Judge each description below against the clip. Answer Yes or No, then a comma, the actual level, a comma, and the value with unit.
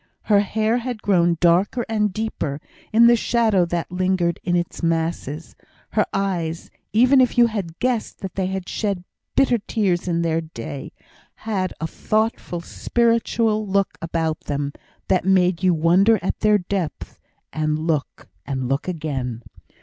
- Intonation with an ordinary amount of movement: Yes, average, 4.5 semitones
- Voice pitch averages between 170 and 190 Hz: Yes, medium, 185 Hz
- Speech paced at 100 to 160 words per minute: Yes, average, 155 wpm